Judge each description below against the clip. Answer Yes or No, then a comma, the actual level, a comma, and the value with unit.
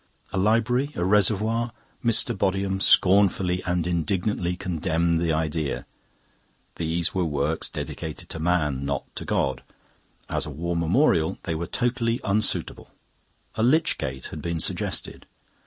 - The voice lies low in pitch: Yes, very low, 90 Hz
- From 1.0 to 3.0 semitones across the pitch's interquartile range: No, average, 4.6 semitones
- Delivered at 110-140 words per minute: Yes, slow, 135 wpm